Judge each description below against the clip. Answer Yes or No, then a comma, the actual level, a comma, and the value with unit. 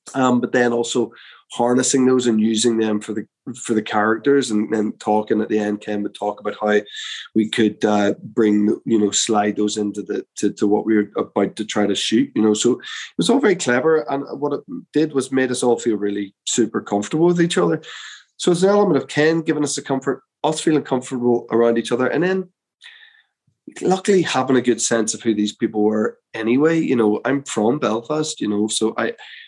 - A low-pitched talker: Yes, low, 120 Hz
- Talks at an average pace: No, fast, 215 wpm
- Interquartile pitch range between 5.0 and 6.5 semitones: Yes, wide, 5.4 semitones